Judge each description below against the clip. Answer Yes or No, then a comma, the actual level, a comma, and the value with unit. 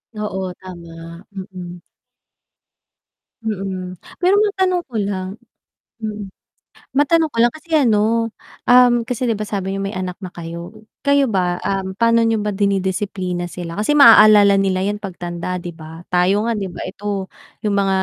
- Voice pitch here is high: Yes, high, 200 Hz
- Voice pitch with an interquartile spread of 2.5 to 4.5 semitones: Yes, average, 3.8 semitones